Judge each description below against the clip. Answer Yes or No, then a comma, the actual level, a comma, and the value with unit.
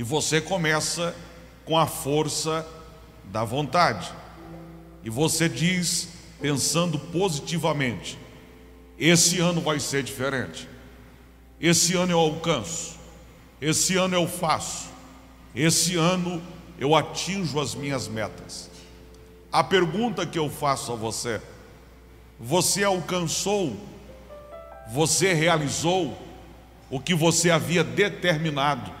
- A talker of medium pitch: Yes, medium, 155 Hz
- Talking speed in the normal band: No, slow, 100 wpm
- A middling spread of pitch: No, wide, 6.2 semitones